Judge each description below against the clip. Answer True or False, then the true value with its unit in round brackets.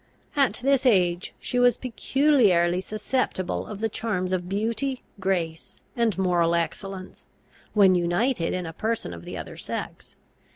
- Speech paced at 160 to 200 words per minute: False (140 wpm)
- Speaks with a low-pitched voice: False (195 Hz)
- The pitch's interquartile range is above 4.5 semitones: True (5.1 semitones)